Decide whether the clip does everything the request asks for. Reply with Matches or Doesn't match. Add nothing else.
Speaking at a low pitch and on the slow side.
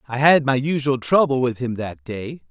Doesn't match